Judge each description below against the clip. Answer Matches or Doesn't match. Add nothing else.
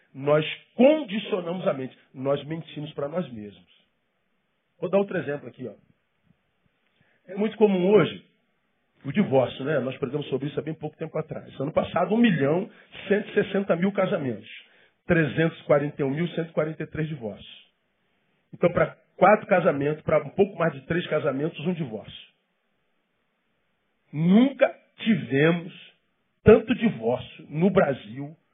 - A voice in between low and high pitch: Matches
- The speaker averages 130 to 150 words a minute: Matches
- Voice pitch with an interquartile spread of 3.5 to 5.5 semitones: Matches